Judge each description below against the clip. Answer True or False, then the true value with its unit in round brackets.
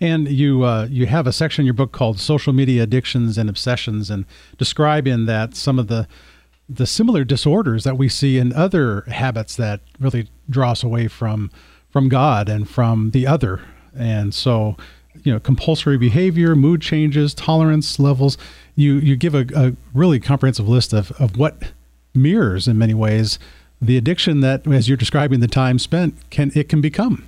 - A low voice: True (130 Hz)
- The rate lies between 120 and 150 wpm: False (180 wpm)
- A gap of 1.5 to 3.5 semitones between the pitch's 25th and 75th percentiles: False (4.5 semitones)